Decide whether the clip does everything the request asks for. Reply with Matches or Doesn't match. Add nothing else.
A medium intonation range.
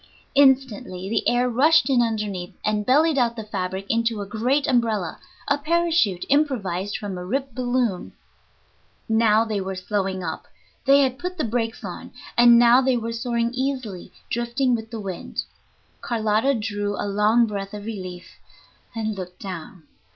Matches